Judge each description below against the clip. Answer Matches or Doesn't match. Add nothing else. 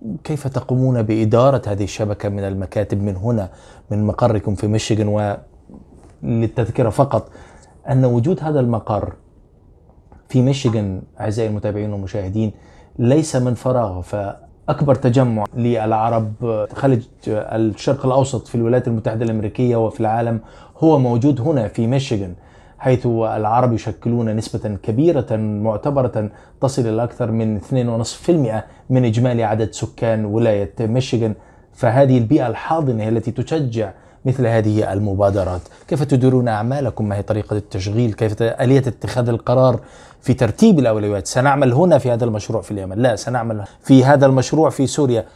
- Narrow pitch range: Doesn't match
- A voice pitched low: Matches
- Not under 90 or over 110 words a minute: Doesn't match